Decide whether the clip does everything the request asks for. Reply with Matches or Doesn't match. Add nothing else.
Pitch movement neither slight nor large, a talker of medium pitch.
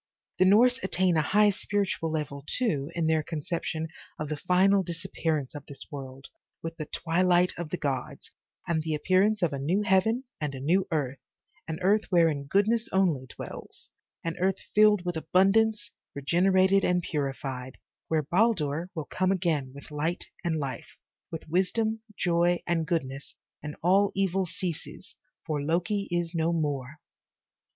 Matches